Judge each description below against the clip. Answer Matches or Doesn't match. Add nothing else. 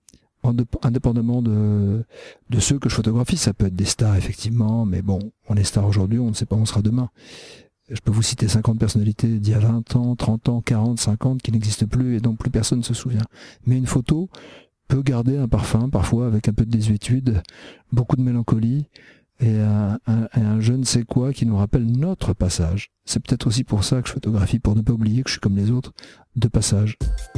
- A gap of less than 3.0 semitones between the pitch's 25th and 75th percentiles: Matches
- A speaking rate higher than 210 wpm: Matches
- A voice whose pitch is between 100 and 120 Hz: Matches